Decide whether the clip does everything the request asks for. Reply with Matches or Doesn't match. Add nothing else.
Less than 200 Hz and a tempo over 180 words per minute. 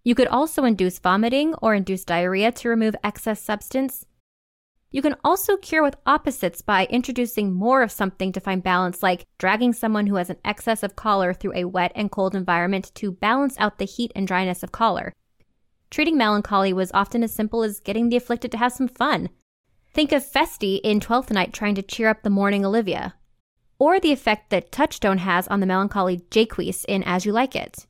Doesn't match